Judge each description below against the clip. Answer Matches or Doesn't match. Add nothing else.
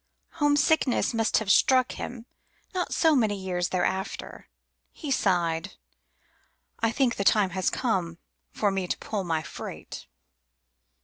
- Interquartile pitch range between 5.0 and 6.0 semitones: Matches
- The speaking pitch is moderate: Doesn't match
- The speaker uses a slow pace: Matches